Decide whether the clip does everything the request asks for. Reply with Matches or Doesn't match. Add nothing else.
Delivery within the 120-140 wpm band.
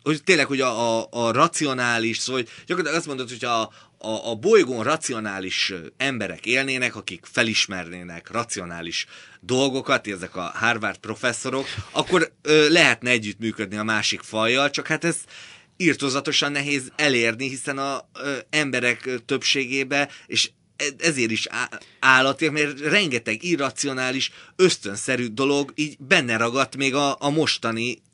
Matches